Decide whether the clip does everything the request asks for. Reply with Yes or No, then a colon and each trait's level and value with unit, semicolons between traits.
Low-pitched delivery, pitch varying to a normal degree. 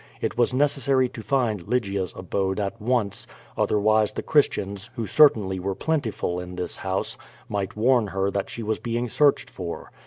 Yes: low, 105 Hz; average, 4.3 semitones